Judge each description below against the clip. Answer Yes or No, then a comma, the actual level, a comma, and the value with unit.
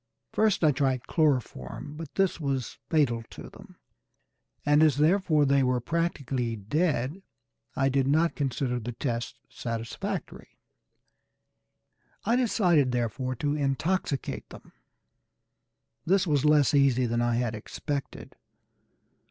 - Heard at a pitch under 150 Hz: Yes, medium, 140 Hz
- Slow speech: Yes, slow, 120 wpm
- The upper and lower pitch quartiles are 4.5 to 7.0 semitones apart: No, average, 4.0 semitones